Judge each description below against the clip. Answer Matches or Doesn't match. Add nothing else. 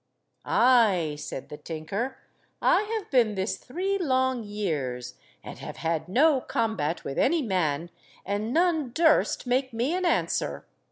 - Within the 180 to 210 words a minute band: Doesn't match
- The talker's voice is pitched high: Matches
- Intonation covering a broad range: Matches